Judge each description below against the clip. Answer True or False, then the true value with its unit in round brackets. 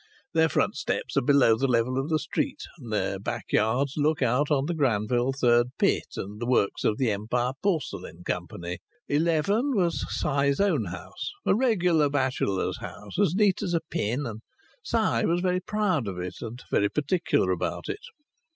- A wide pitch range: True (6.7 semitones)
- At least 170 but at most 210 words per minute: True (175 wpm)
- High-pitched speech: False (140 Hz)